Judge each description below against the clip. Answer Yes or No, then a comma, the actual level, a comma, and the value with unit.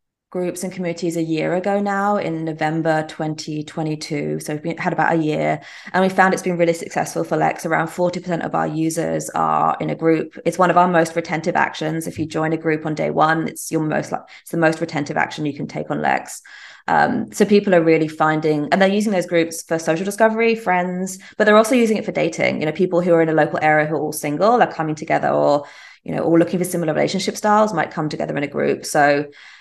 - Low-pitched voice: No, medium, 165 Hz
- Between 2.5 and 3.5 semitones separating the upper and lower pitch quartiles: Yes, average, 2.8 semitones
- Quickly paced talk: Yes, fast, 240 wpm